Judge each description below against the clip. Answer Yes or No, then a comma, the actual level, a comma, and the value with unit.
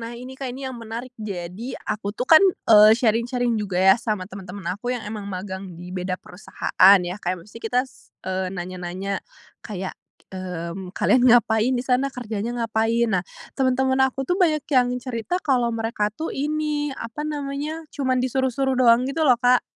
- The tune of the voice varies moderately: Yes, average, 4.7 semitones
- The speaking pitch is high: Yes, high, 235 Hz